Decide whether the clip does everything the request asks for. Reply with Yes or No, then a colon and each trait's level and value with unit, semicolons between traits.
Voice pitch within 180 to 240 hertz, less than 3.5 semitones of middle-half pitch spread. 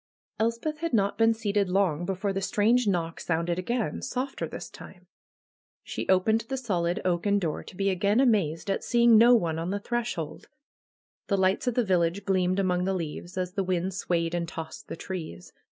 No: high, 190 Hz; average, 4.2 semitones